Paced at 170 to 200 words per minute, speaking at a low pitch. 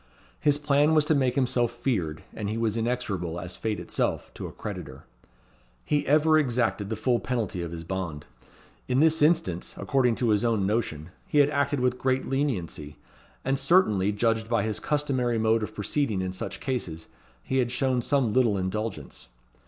Yes: average, 175 wpm; low, 120 Hz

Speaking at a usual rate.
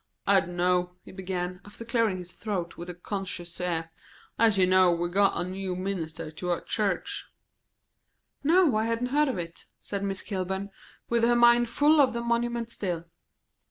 Yes: average, 175 wpm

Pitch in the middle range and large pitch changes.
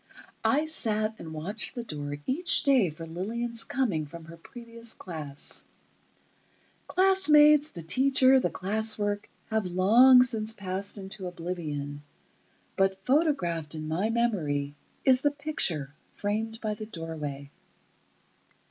No: high, 205 Hz; wide, 7.0 semitones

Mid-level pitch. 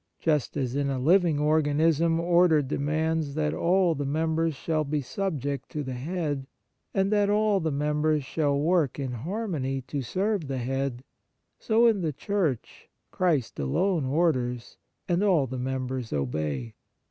Yes: medium, 150 Hz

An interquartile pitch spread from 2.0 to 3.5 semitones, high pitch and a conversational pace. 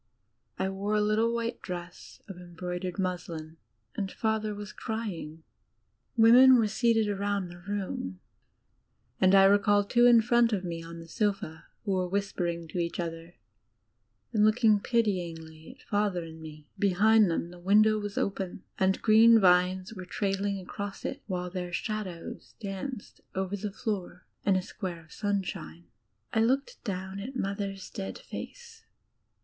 Yes: average, 3.2 semitones; high, 195 Hz; average, 155 wpm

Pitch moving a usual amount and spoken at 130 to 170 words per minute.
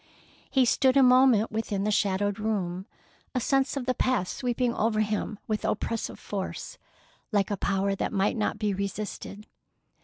Yes: average, 3.6 semitones; average, 160 wpm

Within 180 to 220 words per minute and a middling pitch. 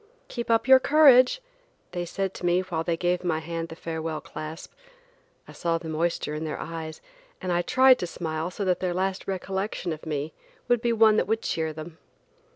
Yes: average, 200 wpm; medium, 175 Hz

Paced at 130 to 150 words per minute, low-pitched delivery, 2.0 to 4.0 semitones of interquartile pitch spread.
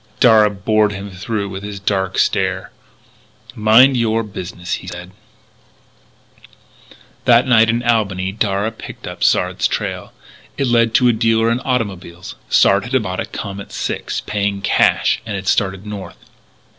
Yes: average, 145 wpm; low, 105 Hz; average, 2.8 semitones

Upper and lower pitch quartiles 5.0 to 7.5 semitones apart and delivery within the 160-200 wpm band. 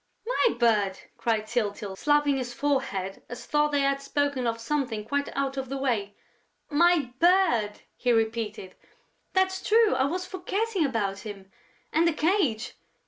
No: wide, 5.4 semitones; average, 150 wpm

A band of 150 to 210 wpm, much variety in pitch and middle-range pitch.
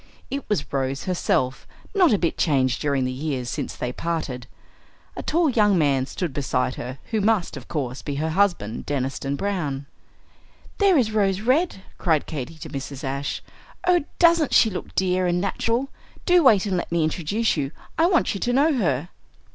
Yes: average, 180 wpm; wide, 8.1 semitones; medium, 170 Hz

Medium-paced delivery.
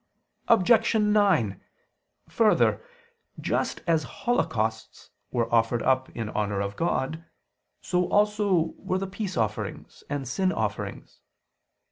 No: slow, 110 wpm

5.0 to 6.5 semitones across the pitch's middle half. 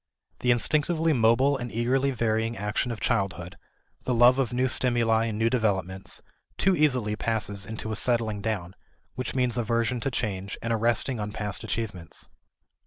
No: average, 3.0 semitones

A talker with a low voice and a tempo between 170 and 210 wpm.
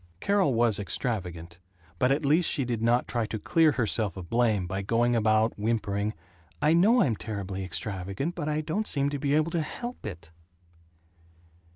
Yes: low, 115 Hz; average, 180 wpm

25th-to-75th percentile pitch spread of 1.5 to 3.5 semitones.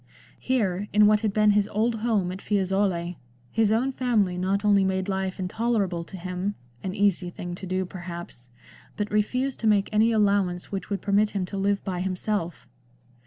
Yes: narrow, 2.5 semitones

